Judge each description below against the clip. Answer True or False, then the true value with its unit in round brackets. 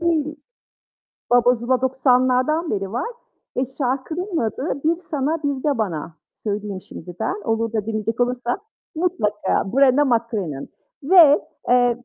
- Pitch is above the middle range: True (250 Hz)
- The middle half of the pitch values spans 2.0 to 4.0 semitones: False (4.7 semitones)